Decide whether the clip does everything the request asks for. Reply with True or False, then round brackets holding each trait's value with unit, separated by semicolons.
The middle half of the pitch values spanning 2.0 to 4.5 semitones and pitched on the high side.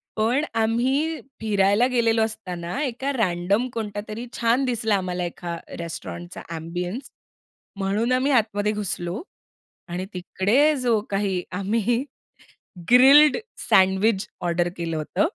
False (5.2 semitones; 210 Hz)